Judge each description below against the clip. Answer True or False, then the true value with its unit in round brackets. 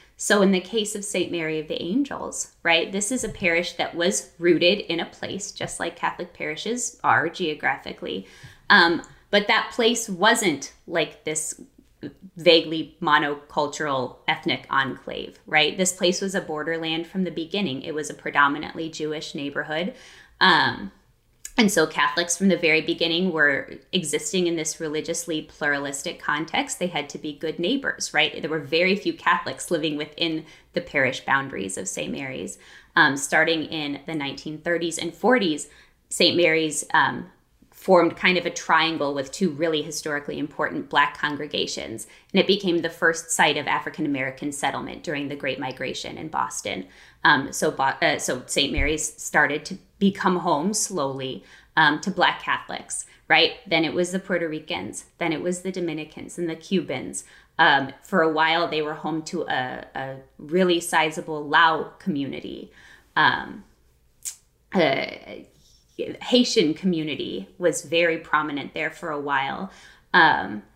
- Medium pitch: True (165 Hz)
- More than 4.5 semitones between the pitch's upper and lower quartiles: False (2.8 semitones)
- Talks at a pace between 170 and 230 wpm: False (155 wpm)